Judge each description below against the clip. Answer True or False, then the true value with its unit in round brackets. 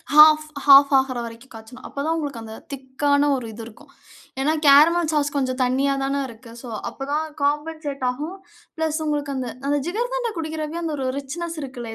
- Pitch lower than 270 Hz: False (285 Hz)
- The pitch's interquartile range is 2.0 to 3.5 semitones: True (3.0 semitones)